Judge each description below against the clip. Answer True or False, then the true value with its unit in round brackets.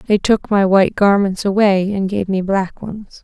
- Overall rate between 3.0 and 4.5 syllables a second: True (4.4 syllables/s)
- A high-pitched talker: True (195 Hz)